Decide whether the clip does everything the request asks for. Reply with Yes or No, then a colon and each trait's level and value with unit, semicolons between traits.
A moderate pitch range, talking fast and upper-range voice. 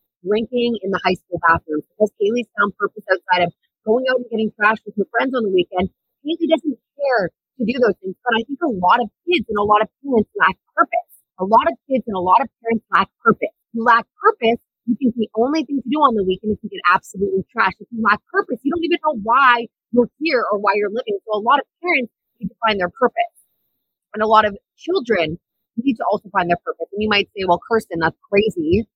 Yes: average, 4.3 semitones; fast, 245 wpm; high, 220 Hz